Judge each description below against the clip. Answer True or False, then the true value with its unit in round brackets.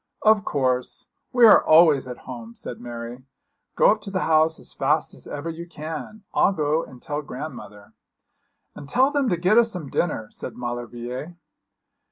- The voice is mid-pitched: True (155 Hz)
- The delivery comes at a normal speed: True (175 wpm)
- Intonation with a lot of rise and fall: True (6.5 semitones)